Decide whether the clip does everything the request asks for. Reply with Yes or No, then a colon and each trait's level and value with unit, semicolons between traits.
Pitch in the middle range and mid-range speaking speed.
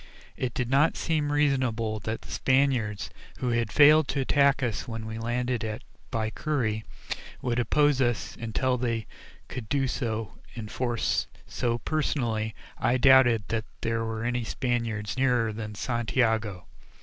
No: low, 120 Hz; average, 145 wpm